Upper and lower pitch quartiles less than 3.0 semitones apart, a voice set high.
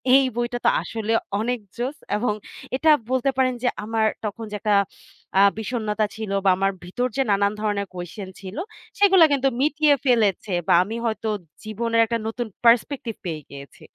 No: average, 3.3 semitones; high, 225 Hz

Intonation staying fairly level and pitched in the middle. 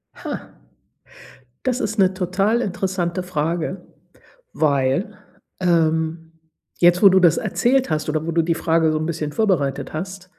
No: average, 3.1 semitones; medium, 175 Hz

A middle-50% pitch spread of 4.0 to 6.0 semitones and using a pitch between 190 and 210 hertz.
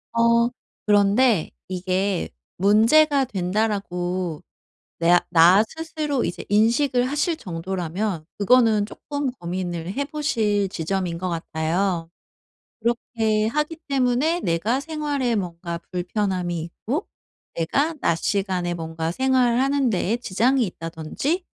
No: wide, 6.4 semitones; high, 205 Hz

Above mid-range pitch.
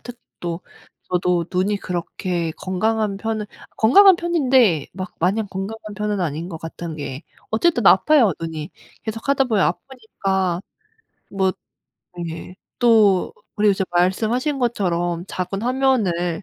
Yes: high, 195 Hz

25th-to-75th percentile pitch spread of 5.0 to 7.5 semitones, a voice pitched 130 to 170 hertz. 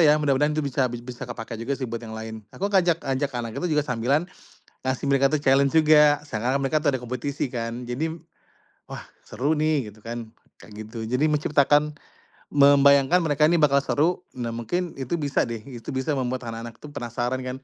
No: average, 3.8 semitones; low, 135 Hz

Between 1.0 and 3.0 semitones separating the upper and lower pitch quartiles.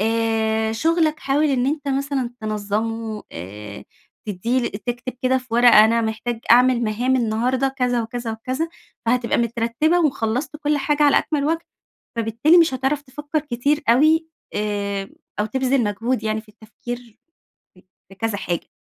No: average, 3.8 semitones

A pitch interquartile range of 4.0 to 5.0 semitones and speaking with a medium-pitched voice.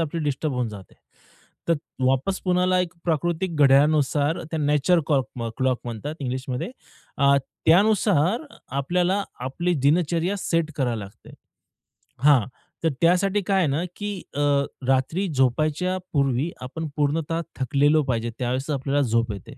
Yes: average, 4.7 semitones; medium, 150 Hz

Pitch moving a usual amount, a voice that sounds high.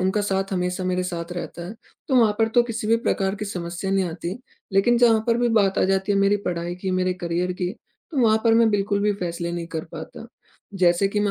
Yes: average, 3.0 semitones; high, 195 Hz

